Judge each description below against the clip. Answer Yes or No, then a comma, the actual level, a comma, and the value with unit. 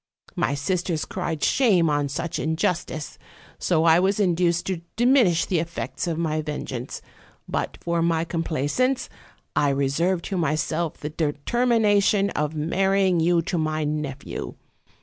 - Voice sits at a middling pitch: Yes, medium, 165 Hz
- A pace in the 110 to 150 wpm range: Yes, average, 140 wpm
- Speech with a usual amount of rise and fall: Yes, average, 3.5 semitones